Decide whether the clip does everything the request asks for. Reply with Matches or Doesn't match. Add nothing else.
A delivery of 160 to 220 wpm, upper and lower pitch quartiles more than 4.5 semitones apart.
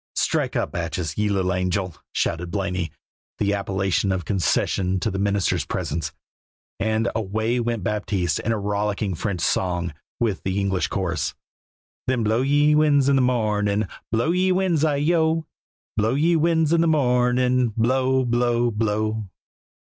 Doesn't match